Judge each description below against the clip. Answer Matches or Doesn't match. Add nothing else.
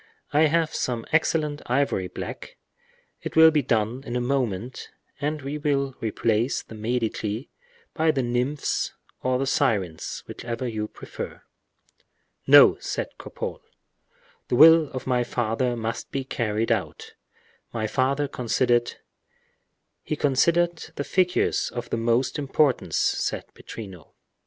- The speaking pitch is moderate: Doesn't match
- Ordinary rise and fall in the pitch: Matches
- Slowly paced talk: Matches